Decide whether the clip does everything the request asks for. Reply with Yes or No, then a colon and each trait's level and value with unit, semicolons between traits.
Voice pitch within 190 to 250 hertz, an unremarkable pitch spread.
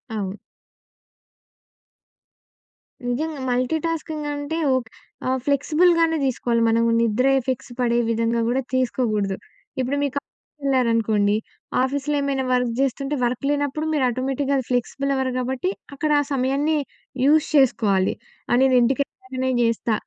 No: very high, 260 Hz; average, 3.2 semitones